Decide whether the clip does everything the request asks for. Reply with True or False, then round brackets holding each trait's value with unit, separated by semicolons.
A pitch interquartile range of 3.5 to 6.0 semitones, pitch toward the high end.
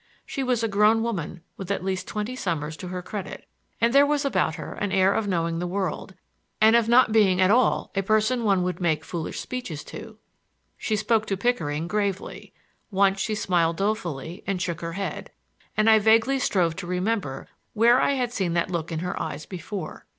True (4.2 semitones; 195 Hz)